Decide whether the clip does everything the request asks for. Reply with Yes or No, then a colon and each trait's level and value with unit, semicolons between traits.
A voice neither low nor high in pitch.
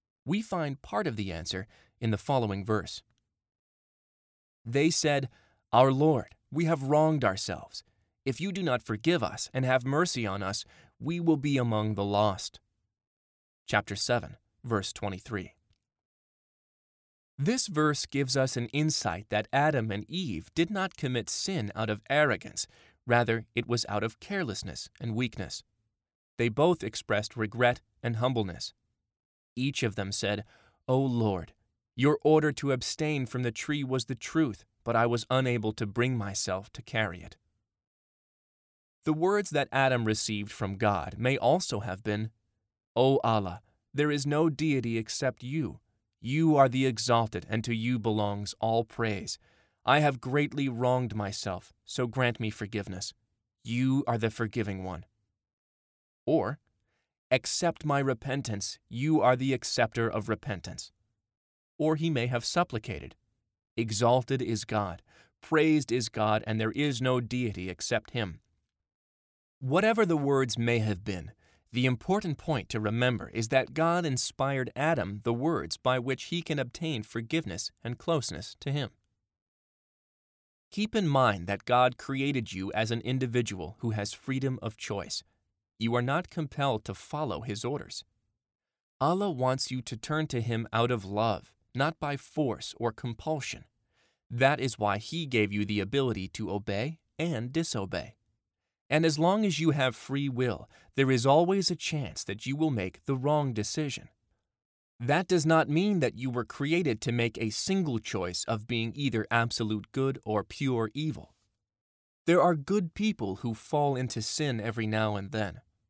No: low, 120 Hz